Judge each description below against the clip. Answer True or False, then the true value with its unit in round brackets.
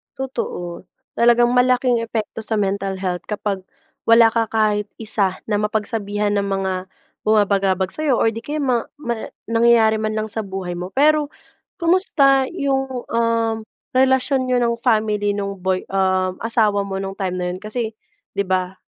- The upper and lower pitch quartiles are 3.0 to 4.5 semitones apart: True (3.6 semitones)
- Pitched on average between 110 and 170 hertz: False (215 Hz)